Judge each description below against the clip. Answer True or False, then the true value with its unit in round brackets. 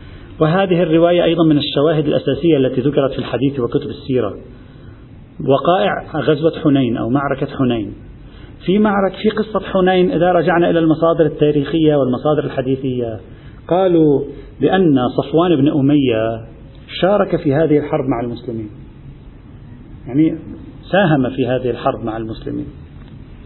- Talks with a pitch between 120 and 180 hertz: True (140 Hz)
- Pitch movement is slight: False (4.4 semitones)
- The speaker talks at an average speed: True (125 wpm)